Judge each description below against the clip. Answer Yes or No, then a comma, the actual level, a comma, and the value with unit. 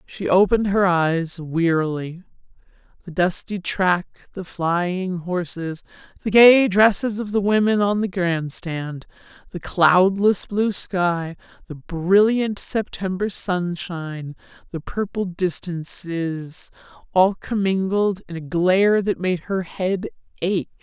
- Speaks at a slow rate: Yes, slow, 120 wpm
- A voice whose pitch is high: No, medium, 180 Hz